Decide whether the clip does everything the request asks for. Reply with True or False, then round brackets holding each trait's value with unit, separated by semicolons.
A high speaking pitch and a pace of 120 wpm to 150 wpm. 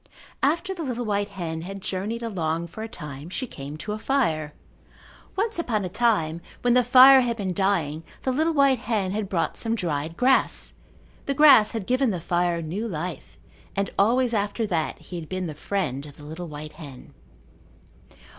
False (200 Hz; 185 wpm)